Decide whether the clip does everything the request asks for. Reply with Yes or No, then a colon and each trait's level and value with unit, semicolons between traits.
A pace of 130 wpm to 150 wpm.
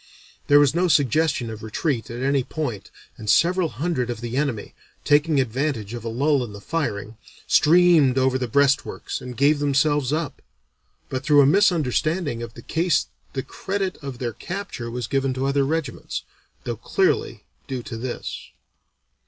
No: average, 165 wpm